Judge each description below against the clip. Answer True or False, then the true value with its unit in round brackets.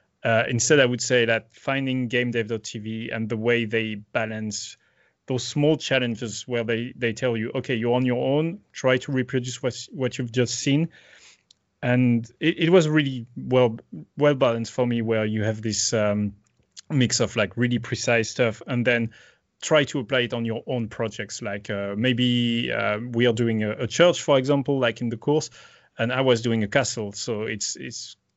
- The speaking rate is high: False (190 wpm)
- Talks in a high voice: False (120 Hz)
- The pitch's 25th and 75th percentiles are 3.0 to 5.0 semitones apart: False (2.4 semitones)